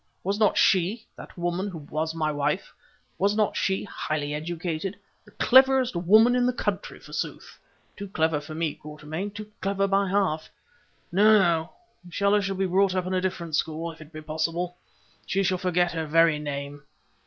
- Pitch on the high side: No, medium, 175 Hz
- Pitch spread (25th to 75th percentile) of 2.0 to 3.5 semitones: No, average, 3.9 semitones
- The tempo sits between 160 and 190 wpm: Yes, average, 165 wpm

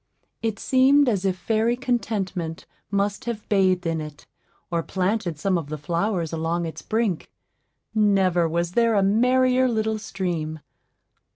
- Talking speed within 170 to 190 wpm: No, average, 145 wpm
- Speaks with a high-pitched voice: Yes, high, 195 Hz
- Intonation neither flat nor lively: Yes, average, 4.6 semitones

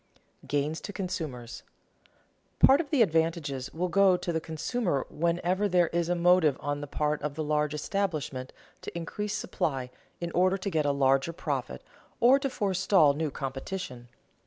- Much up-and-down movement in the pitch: No, average, 4.4 semitones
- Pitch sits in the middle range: Yes, medium, 165 Hz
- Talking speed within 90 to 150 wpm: No, average, 165 wpm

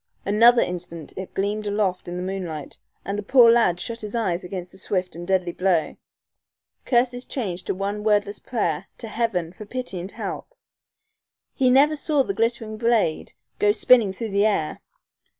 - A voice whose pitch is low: No, high, 205 Hz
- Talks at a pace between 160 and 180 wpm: Yes, average, 170 wpm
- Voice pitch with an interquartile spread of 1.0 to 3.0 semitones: No, average, 4.3 semitones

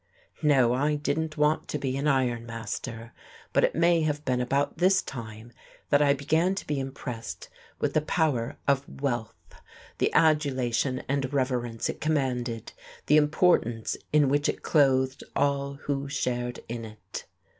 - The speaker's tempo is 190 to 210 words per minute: No, average, 155 wpm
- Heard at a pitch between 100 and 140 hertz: Yes, low, 135 Hz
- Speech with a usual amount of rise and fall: Yes, average, 3.4 semitones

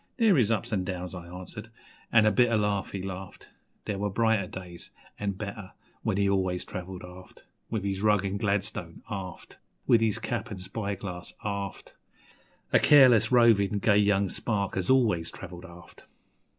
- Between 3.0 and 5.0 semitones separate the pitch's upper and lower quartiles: No, narrow, 2.6 semitones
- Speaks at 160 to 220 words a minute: Yes, average, 165 wpm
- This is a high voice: No, low, 100 Hz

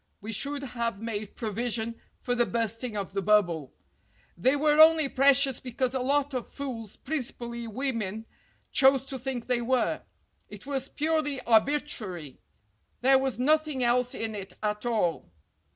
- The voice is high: Yes, high, 245 Hz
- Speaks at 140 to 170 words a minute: Yes, average, 150 wpm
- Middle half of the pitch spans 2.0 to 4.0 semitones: Yes, average, 3.7 semitones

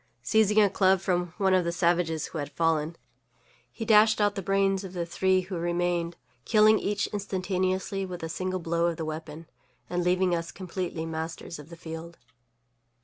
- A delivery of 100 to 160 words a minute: No, average, 180 wpm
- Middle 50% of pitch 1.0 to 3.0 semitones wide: Yes, narrow, 2.5 semitones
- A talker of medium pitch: Yes, medium, 175 Hz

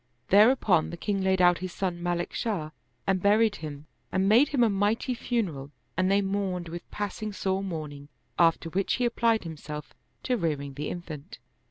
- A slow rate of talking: No, average, 175 wpm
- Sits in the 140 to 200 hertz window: Yes, high, 190 Hz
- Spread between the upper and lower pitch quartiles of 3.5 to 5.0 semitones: Yes, average, 4.0 semitones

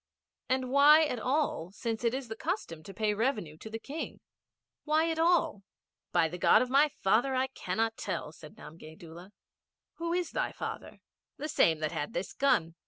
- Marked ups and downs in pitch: Yes, wide, 8.7 semitones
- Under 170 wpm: No, average, 190 wpm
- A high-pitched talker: Yes, high, 235 Hz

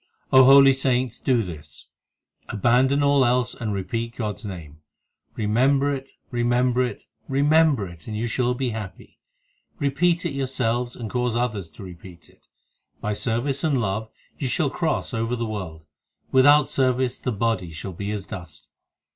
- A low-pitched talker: Yes, low, 120 Hz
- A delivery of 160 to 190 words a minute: Yes, average, 165 wpm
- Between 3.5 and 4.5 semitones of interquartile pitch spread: Yes, average, 4.2 semitones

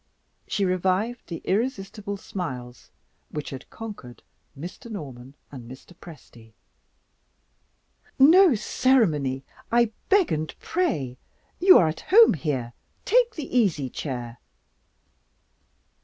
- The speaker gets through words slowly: Yes, slow, 105 wpm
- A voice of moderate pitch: Yes, medium, 180 Hz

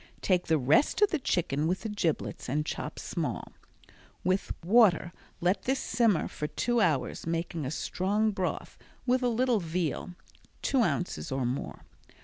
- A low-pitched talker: No, medium, 180 Hz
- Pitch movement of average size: No, wide, 6.0 semitones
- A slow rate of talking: No, average, 155 wpm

